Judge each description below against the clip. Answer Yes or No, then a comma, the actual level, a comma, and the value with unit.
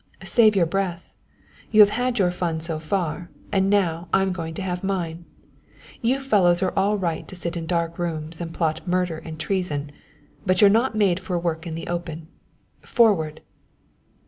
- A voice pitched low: No, medium, 175 Hz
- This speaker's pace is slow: No, average, 170 wpm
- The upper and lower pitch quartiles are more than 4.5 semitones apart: No, average, 2.9 semitones